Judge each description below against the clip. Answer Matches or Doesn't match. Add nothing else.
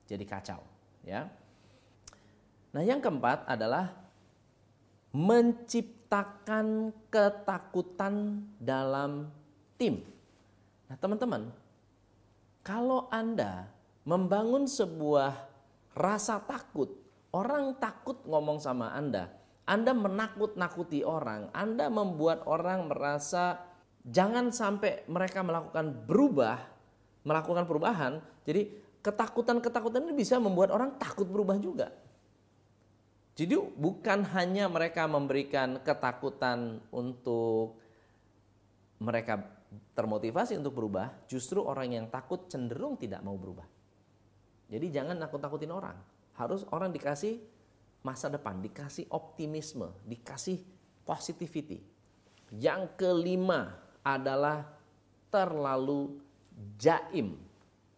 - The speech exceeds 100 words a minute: Doesn't match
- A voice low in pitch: Doesn't match